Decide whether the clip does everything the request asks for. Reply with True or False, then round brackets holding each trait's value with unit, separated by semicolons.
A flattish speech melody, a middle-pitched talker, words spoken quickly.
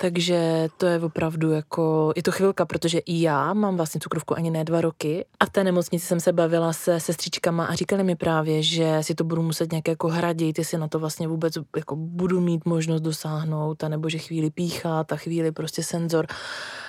True (1.4 semitones; 165 Hz; 205 wpm)